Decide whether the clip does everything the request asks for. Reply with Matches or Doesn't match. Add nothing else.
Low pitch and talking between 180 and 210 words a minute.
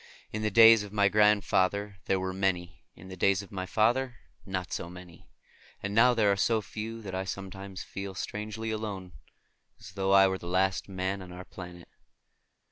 Matches